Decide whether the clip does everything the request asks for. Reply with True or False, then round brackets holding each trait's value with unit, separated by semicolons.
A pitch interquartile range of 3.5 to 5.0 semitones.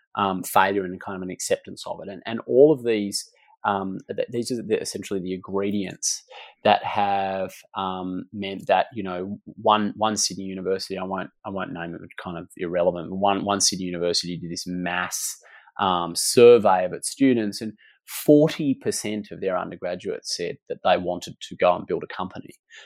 False (2.6 semitones)